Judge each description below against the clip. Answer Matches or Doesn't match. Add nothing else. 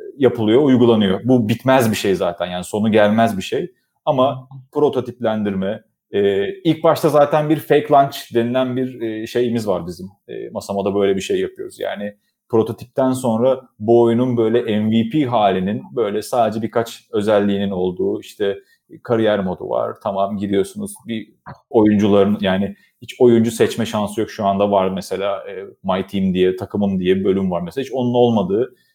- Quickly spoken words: Matches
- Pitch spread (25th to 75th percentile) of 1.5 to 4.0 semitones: Doesn't match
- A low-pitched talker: Matches